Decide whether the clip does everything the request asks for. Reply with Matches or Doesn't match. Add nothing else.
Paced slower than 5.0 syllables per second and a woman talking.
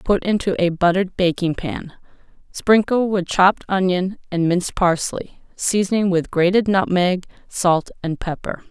Matches